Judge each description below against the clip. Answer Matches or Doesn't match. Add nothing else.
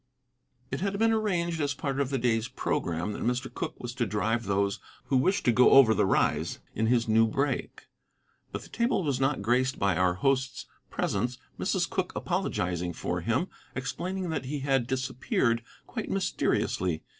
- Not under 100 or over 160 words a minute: Doesn't match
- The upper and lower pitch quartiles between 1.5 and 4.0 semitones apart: Doesn't match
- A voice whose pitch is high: Doesn't match